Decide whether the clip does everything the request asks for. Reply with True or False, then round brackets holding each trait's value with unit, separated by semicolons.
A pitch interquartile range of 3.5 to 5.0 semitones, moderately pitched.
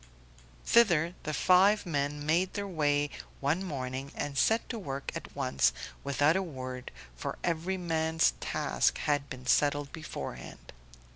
True (4.3 semitones; 150 Hz)